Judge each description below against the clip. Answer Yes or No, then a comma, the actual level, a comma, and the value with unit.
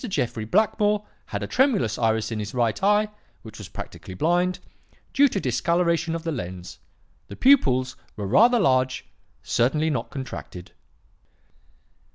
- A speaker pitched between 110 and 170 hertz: Yes, low, 135 Hz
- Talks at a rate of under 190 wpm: Yes, average, 140 wpm